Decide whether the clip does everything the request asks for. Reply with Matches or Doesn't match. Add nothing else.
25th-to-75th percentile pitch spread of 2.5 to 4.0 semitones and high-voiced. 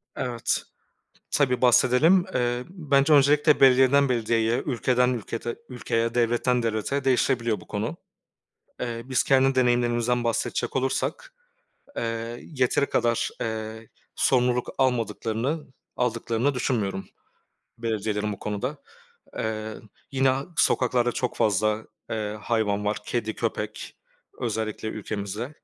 Doesn't match